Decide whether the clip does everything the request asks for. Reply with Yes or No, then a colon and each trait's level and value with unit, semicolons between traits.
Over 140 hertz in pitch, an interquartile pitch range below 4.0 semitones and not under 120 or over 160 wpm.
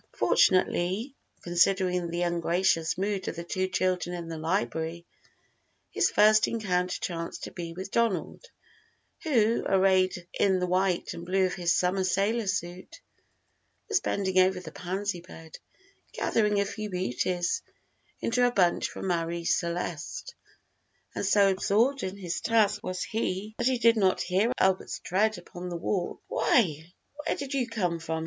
Yes: medium, 185 Hz; average, 3.1 semitones; average, 155 wpm